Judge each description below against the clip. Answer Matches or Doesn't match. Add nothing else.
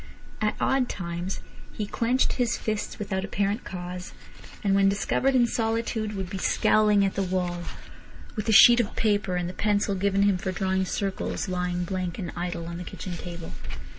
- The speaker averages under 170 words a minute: Doesn't match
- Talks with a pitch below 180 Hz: Doesn't match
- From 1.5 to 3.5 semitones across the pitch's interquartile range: Matches